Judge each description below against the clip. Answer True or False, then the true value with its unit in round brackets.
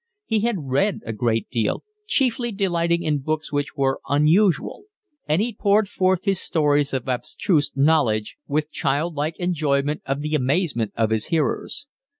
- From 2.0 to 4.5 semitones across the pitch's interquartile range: False (5.1 semitones)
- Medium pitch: True (150 Hz)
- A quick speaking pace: False (155 wpm)